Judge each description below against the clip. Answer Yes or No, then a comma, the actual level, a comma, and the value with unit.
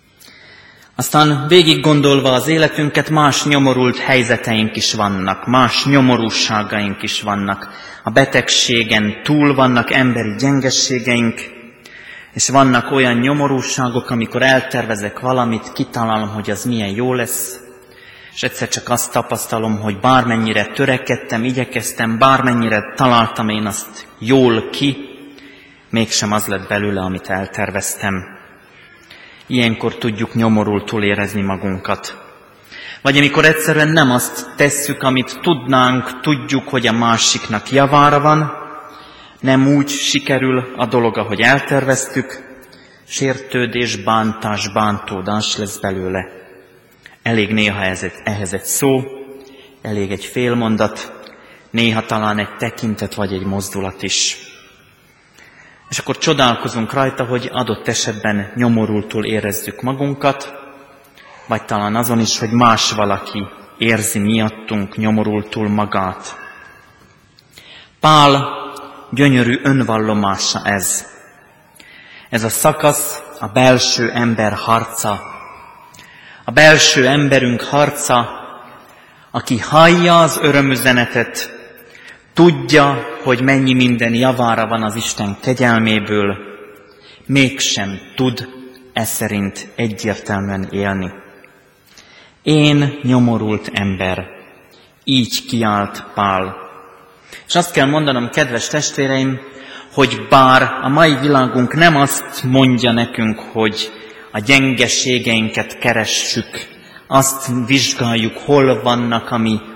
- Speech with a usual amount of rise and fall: Yes, average, 4.0 semitones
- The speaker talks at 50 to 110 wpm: Yes, slow, 105 wpm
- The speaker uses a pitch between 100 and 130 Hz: Yes, low, 120 Hz